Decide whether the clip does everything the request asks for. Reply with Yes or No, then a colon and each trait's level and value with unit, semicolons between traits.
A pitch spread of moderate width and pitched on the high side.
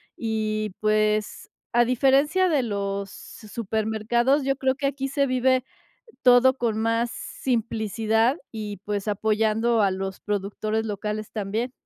Yes: average, 3.0 semitones; high, 220 Hz